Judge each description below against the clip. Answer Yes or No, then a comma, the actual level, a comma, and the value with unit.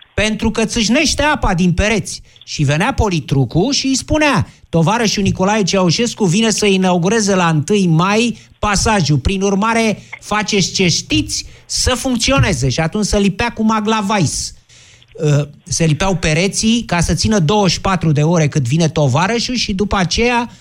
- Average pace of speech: Yes, average, 145 wpm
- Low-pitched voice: No, high, 195 Hz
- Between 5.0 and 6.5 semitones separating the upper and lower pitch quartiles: Yes, wide, 5.4 semitones